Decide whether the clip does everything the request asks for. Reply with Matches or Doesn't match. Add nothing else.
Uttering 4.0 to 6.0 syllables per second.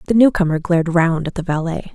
Doesn't match